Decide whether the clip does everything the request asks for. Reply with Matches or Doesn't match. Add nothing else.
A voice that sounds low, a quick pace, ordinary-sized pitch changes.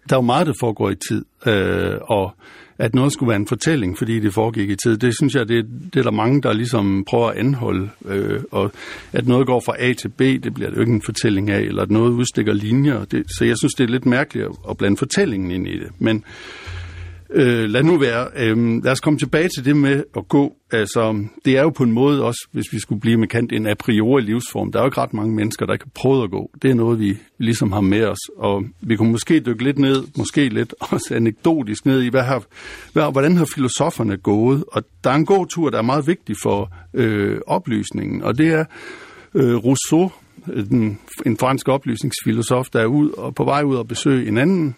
Matches